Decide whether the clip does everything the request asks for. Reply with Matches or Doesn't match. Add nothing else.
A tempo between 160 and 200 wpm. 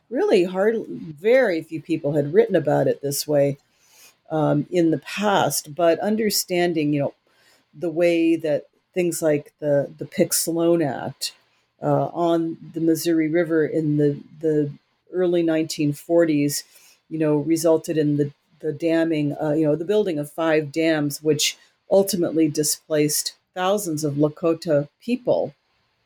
Doesn't match